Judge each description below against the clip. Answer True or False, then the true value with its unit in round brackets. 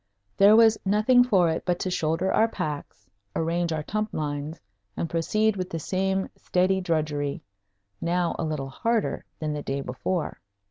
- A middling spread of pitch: True (4.1 semitones)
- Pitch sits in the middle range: True (175 Hz)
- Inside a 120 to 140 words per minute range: False (165 wpm)